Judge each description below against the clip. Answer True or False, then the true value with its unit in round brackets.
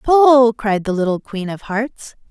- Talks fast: False (180 wpm)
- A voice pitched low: False (230 Hz)